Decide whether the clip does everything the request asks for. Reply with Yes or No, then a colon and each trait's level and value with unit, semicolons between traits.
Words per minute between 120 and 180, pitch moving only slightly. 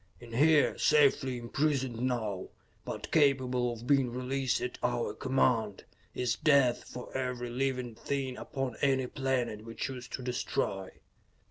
Yes: slow, 135 wpm; narrow, 2.0 semitones